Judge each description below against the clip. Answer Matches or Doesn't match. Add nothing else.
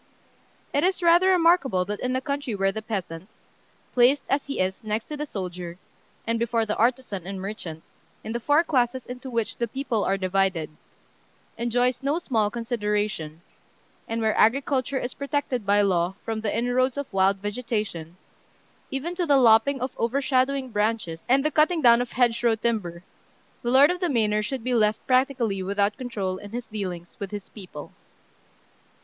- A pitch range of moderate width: Matches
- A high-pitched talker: Matches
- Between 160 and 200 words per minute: Matches